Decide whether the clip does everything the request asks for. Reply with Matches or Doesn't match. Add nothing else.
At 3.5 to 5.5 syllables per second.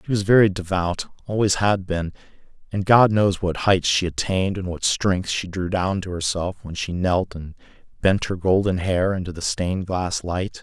Matches